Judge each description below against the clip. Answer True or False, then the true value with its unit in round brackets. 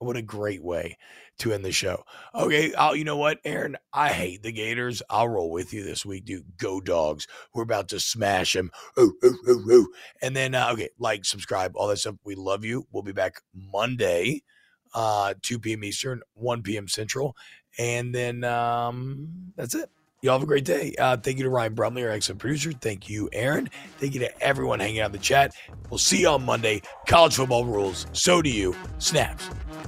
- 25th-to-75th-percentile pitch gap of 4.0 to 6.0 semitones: True (5.0 semitones)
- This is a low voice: True (120 Hz)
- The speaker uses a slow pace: False (200 wpm)